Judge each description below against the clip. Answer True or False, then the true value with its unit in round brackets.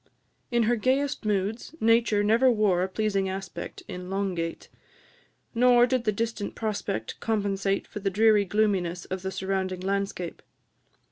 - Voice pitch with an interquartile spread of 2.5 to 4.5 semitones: True (2.9 semitones)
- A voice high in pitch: True (205 Hz)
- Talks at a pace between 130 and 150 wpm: True (145 wpm)